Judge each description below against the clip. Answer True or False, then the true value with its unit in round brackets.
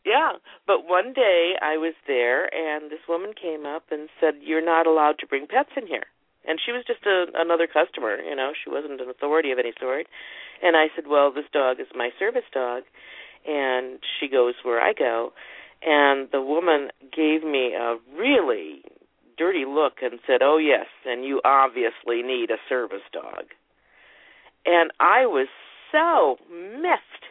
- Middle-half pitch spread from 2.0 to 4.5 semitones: False (4.9 semitones)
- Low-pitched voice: False (155 Hz)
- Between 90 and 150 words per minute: False (175 wpm)